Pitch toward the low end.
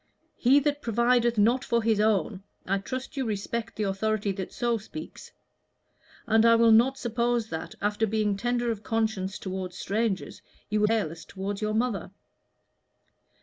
No: high, 220 Hz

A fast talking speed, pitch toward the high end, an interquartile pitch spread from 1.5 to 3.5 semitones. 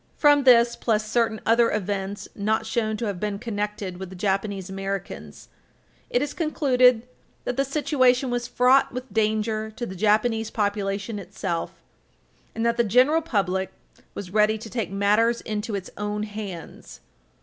No: average, 155 wpm; high, 215 Hz; average, 3.0 semitones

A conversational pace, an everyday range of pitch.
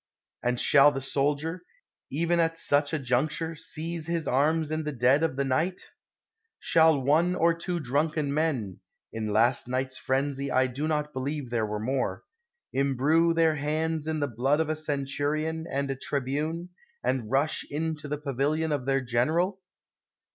Yes: average, 165 wpm; average, 3.2 semitones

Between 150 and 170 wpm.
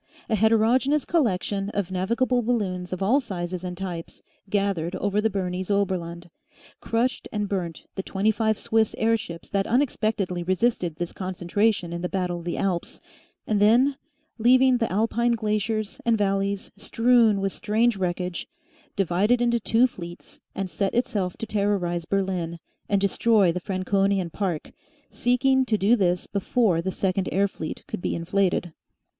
Yes: average, 155 wpm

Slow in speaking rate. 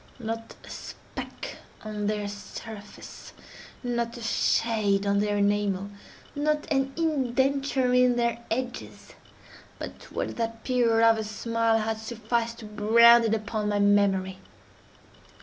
Yes: slow, 115 wpm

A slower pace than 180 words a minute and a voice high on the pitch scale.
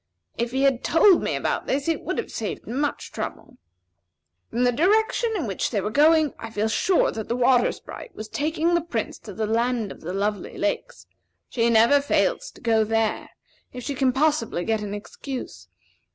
No: average, 195 wpm; high, 245 Hz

